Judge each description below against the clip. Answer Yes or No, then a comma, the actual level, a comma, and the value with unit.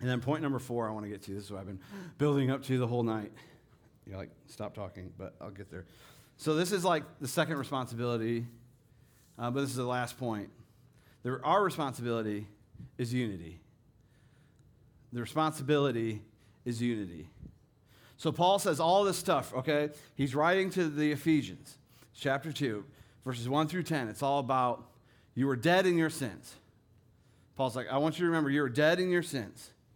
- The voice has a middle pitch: No, low, 130 Hz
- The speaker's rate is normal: Yes, average, 185 wpm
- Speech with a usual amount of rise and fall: Yes, average, 4.4 semitones